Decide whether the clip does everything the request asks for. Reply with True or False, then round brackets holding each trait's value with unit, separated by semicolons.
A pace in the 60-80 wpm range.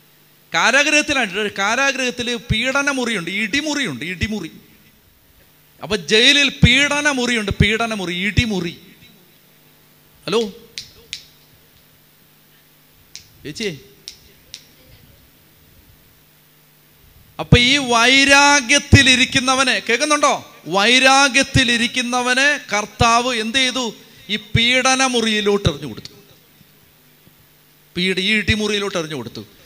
True (65 wpm)